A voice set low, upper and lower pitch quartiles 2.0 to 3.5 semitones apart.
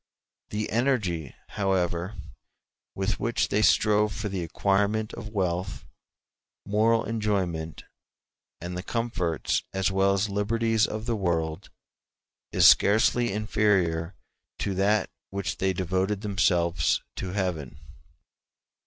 Yes: low, 100 Hz; average, 3.1 semitones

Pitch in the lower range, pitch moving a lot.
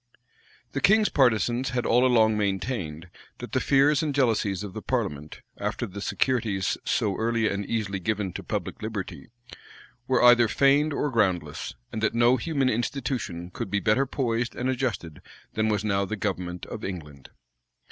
No: low, 110 Hz; average, 4.6 semitones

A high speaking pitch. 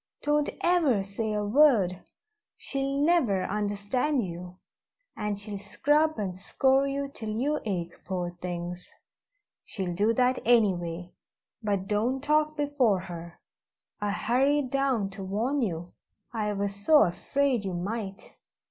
Yes: high, 210 Hz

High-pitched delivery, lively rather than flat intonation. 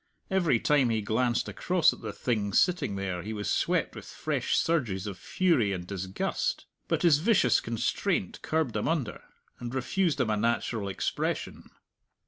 No: low, 120 Hz; wide, 7.4 semitones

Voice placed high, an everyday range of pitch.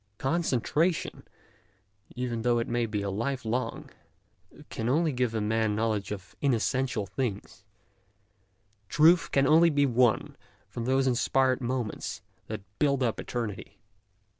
No: low, 125 Hz; average, 3.3 semitones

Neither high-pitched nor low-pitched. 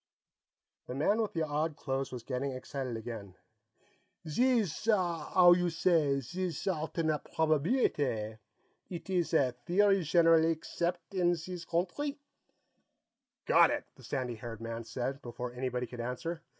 Yes: medium, 155 Hz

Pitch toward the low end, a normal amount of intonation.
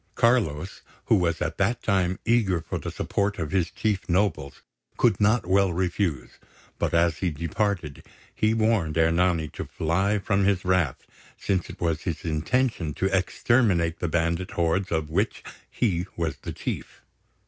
Yes: very low, 90 Hz; average, 3.4 semitones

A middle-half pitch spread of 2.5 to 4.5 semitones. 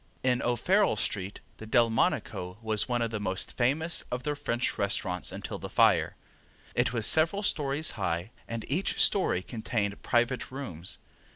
No: average, 4.9 semitones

